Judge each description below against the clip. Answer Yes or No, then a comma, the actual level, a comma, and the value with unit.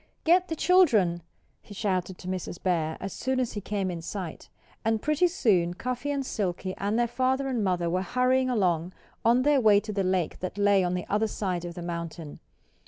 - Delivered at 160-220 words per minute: Yes, fast, 205 wpm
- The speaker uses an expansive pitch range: Yes, wide, 5.9 semitones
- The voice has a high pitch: Yes, high, 200 Hz